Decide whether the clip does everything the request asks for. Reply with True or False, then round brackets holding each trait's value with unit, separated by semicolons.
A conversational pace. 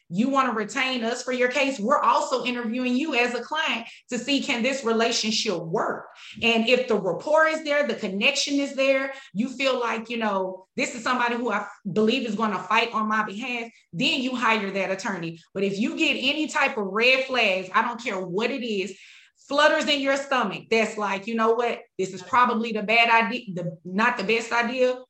False (215 wpm)